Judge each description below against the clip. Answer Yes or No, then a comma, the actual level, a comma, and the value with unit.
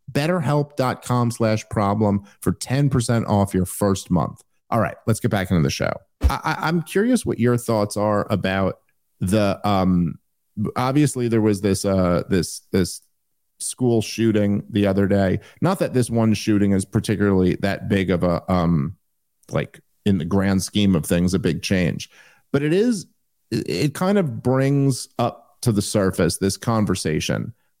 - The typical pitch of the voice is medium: No, low, 105 Hz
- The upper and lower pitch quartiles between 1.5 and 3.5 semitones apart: No, average, 4.6 semitones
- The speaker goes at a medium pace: Yes, average, 160 wpm